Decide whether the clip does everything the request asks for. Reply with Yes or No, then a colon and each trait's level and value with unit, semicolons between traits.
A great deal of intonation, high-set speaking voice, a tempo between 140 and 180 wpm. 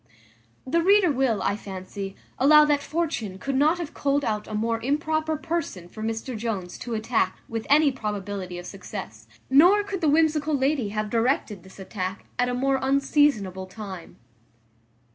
Yes: wide, 6.5 semitones; high, 245 Hz; average, 160 wpm